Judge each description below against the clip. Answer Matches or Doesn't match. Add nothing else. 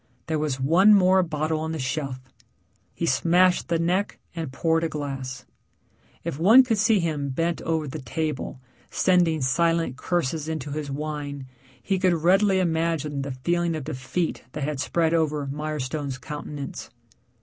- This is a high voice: Doesn't match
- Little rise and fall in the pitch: Doesn't match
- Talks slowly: Doesn't match